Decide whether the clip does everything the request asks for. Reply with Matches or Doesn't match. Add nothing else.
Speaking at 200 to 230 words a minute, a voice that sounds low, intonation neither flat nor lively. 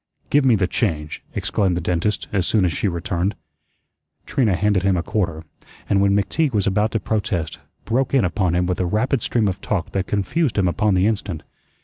Matches